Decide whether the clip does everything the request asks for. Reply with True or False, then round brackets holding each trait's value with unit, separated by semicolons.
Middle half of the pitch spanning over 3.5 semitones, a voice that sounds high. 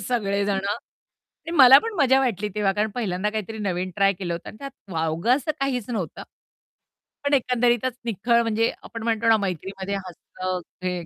True (4.2 semitones; 210 Hz)